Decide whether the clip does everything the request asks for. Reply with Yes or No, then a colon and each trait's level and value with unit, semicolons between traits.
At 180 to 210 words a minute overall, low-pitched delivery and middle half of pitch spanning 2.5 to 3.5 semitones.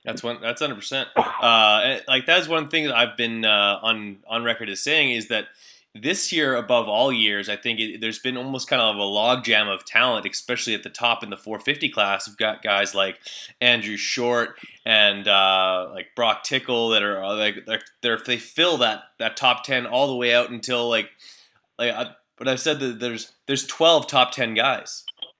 Yes: fast, 205 wpm; low, 120 Hz; average, 3.2 semitones